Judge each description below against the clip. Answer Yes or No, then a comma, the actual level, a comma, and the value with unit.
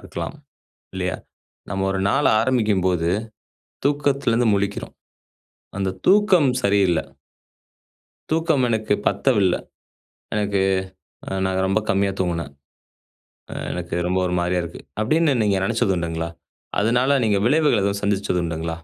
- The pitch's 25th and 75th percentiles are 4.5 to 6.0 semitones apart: Yes, average, 5.2 semitones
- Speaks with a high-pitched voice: No, low, 100 Hz